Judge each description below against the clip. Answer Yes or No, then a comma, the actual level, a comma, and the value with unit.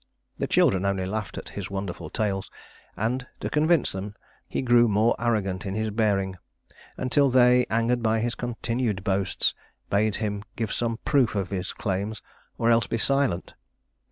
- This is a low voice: Yes, low, 110 Hz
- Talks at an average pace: Yes, average, 160 wpm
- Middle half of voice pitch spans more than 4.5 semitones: No, average, 3.4 semitones